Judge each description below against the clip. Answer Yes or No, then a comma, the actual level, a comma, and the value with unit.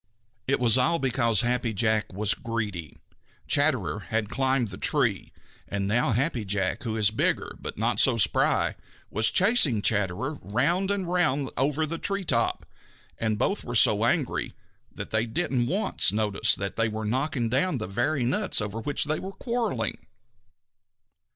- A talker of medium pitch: No, low, 120 Hz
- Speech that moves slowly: No, average, 165 wpm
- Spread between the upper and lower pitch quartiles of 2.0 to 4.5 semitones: No, average, 5.3 semitones